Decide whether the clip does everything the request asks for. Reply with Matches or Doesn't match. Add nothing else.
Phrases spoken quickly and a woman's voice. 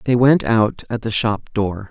Doesn't match